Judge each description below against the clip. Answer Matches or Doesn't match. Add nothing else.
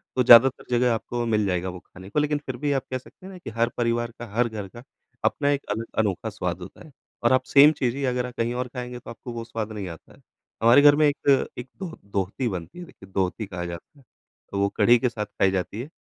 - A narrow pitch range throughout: Doesn't match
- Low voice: Matches